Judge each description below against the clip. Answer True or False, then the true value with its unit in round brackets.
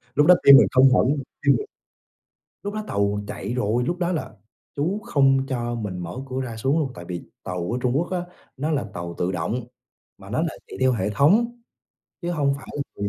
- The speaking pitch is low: True (130 Hz)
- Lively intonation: True (6.6 semitones)